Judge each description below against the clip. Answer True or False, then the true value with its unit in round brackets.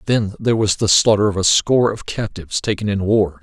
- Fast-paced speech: True (230 wpm)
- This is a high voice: False (105 Hz)